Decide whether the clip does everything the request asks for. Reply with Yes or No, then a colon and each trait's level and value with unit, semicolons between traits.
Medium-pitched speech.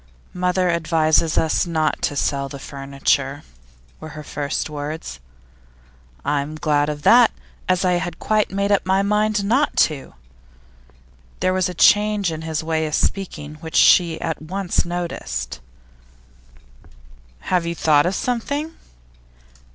Yes: medium, 165 Hz